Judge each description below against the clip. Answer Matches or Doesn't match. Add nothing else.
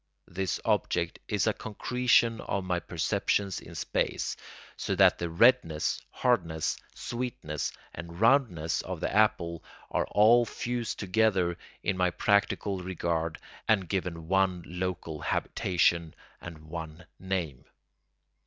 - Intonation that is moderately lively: Matches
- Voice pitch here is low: Matches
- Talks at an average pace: Doesn't match